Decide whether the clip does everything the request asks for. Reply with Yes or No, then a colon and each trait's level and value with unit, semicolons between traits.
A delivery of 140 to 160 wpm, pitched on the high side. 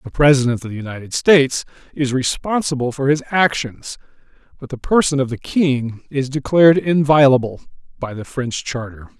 No: average, 155 wpm; low, 135 Hz